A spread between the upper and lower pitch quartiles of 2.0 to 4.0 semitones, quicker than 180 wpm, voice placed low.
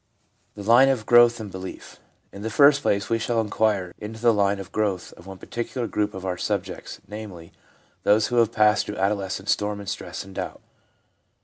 Yes: average, 2.7 semitones; average, 195 wpm; low, 105 Hz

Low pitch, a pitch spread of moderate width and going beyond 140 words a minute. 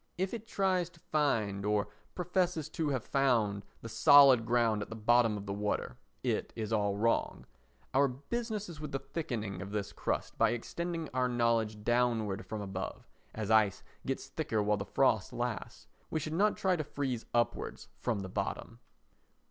No: low, 120 Hz; wide, 6.5 semitones; average, 175 wpm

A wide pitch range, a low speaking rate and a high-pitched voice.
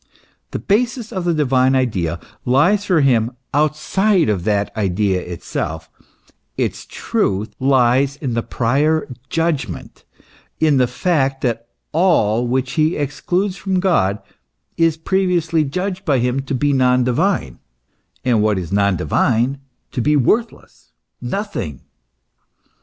No: wide, 6.4 semitones; slow, 130 wpm; low, 135 Hz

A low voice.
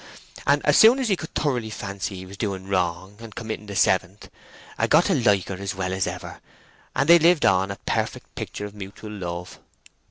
Yes: low, 100 Hz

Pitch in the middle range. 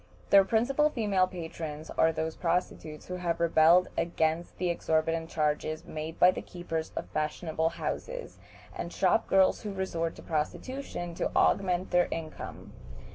Yes: medium, 170 Hz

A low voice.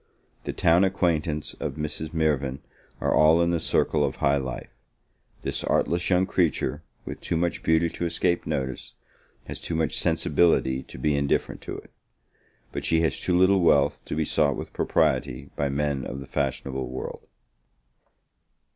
Yes: very low, 75 Hz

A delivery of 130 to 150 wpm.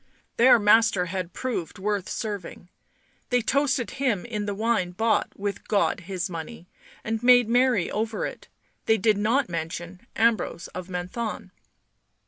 Yes: average, 140 wpm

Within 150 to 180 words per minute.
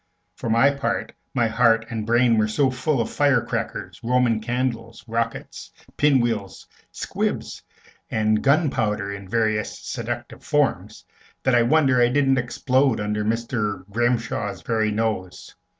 No: slow, 135 wpm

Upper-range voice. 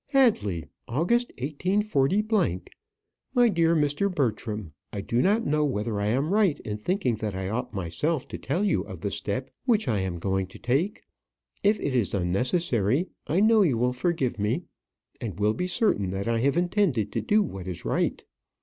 No: low, 130 Hz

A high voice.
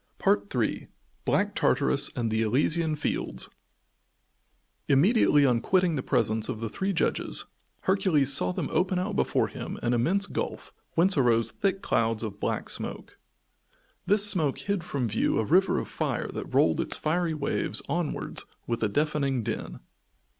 No: medium, 145 Hz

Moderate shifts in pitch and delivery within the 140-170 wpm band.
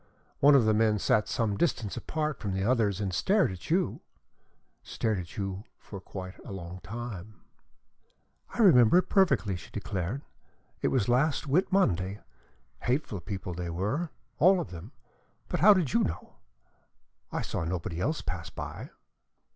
No: wide, 7.2 semitones; average, 160 wpm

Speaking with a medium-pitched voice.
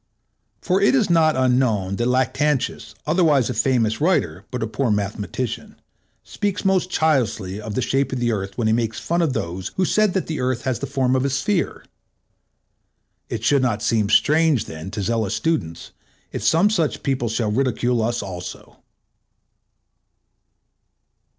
No: low, 125 Hz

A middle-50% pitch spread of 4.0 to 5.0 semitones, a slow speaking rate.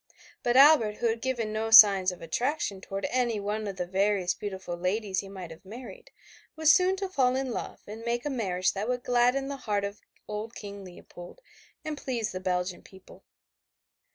No: average, 4.5 semitones; average, 190 wpm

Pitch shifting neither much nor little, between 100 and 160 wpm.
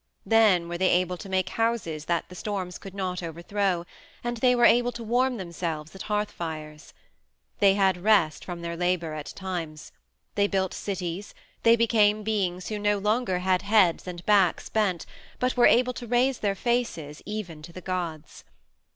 No: average, 3.8 semitones; average, 175 wpm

